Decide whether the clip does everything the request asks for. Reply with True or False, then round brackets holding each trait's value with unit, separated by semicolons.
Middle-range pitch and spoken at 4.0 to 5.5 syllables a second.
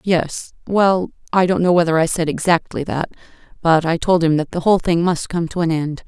True (170 Hz; 5.2 syllables/s)